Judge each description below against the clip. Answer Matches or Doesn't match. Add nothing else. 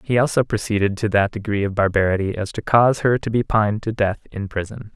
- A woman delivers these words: Doesn't match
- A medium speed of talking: Doesn't match